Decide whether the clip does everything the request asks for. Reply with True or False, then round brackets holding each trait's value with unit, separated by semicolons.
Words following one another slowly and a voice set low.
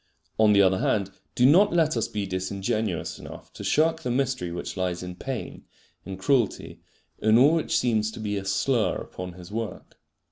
False (185 wpm; 110 Hz)